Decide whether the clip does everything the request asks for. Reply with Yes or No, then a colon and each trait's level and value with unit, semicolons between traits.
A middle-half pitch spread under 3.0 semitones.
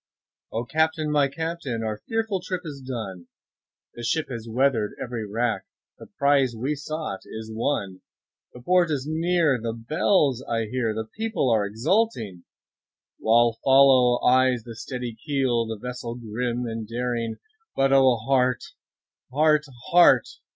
No: average, 4.4 semitones